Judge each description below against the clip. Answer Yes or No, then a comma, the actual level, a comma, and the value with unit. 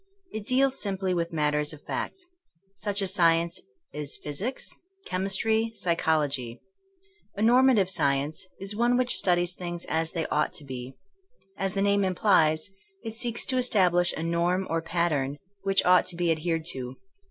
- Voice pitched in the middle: Yes, medium, 175 Hz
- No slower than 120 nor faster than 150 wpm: No, average, 165 wpm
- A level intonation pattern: No, average, 4.2 semitones